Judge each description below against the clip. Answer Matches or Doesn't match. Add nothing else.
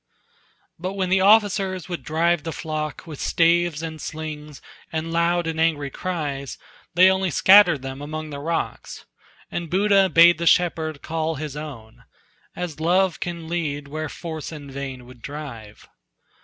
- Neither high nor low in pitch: Matches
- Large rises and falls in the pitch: Doesn't match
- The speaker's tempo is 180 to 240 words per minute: Doesn't match